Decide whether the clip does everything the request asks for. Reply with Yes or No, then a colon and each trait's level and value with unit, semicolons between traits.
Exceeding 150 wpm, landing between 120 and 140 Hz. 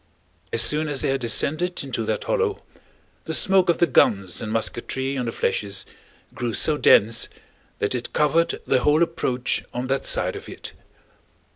Yes: average, 170 wpm; low, 135 Hz